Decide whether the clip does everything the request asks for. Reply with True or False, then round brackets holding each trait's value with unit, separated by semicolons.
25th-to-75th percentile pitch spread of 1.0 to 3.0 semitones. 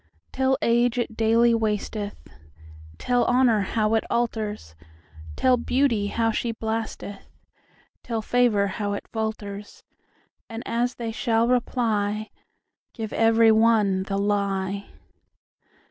True (2.5 semitones)